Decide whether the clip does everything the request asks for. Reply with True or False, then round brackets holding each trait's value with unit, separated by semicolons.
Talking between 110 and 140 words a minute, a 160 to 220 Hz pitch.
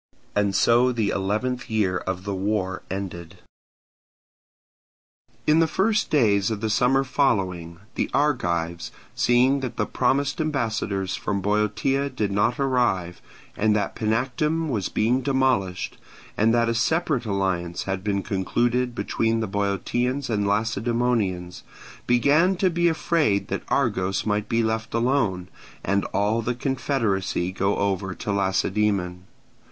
False (135 wpm; 110 Hz)